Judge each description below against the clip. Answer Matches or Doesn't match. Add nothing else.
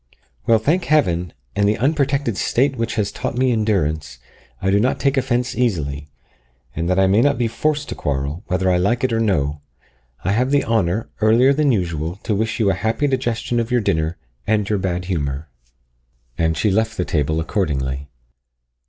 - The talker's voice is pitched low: Matches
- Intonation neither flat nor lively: Doesn't match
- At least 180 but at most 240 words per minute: Matches